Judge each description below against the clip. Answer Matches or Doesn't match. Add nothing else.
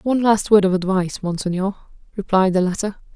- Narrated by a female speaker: Matches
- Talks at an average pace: Matches